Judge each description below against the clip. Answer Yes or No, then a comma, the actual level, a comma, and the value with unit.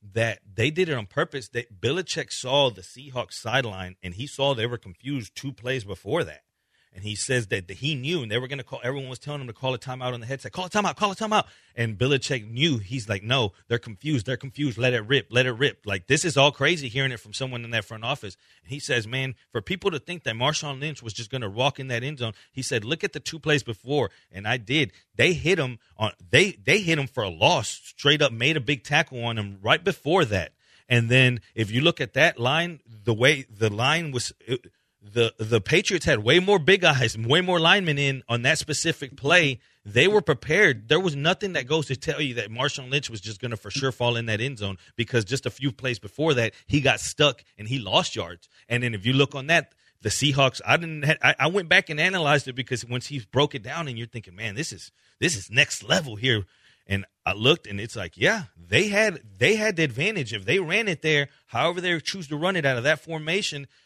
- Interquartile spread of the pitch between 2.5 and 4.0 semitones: No, average, 4.6 semitones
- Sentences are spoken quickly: Yes, fast, 250 wpm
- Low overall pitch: Yes, low, 130 Hz